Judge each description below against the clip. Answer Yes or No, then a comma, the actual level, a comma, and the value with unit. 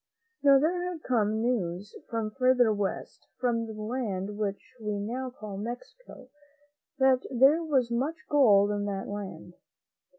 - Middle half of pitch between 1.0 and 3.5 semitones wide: No, average, 4.2 semitones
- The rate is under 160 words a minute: Yes, average, 140 wpm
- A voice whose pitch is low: No, high, 230 Hz